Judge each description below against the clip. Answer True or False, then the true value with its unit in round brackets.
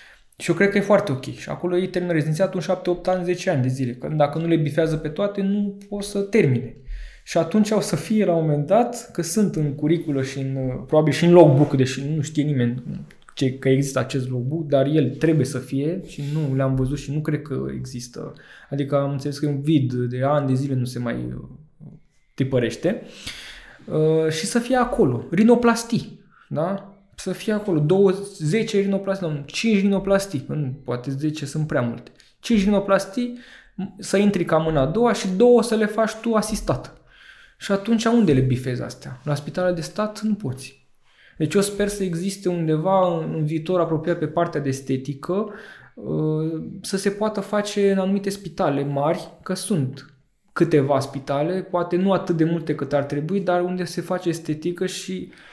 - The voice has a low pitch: False (165 Hz)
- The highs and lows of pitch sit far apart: True (5.7 semitones)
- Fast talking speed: True (190 wpm)